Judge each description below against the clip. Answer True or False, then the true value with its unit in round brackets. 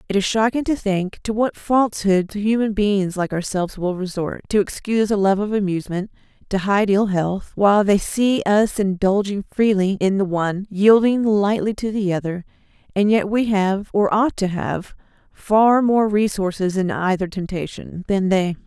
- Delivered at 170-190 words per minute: True (175 wpm)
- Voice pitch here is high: True (200 Hz)